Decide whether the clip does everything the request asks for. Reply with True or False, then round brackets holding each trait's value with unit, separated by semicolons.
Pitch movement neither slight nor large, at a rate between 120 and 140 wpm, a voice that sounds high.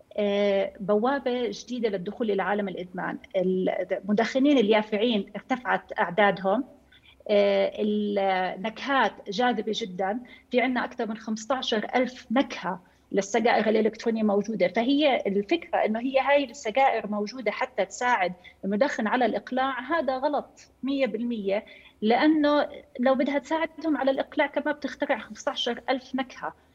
False (4.5 semitones; 110 wpm; 235 Hz)